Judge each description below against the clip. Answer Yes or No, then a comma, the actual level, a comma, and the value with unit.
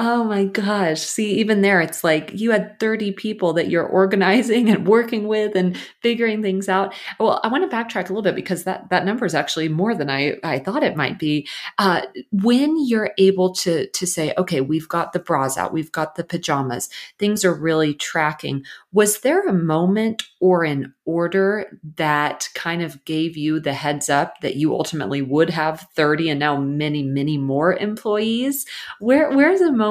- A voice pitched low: No, medium, 180 Hz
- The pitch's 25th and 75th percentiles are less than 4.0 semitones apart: No, average, 5.3 semitones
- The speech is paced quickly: No, average, 195 wpm